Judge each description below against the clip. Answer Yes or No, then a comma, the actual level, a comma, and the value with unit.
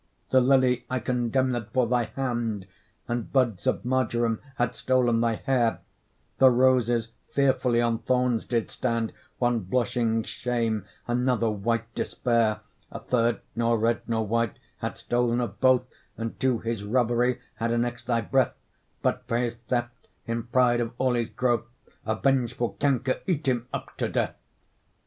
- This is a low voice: Yes, low, 120 Hz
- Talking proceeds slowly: No, average, 155 wpm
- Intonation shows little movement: Yes, narrow, 1.6 semitones